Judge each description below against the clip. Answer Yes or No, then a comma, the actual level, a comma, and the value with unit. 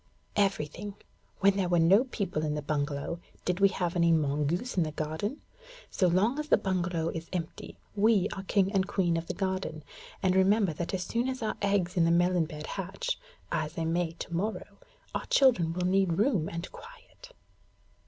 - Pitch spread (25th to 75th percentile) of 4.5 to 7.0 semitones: No, average, 3.3 semitones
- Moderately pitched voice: Yes, medium, 180 Hz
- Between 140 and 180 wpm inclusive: No, average, 190 wpm